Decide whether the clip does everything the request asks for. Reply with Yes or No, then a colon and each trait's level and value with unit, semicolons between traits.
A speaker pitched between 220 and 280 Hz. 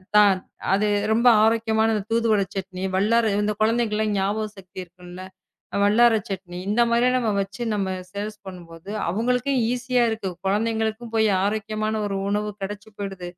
No: high, 210 Hz